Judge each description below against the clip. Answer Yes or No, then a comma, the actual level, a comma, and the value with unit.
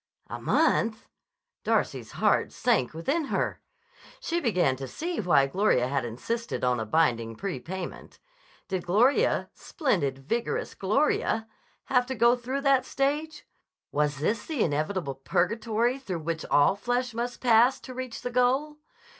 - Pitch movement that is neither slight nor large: No, wide, 8.5 semitones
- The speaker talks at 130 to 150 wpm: Yes, average, 140 wpm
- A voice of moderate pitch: No, high, 220 Hz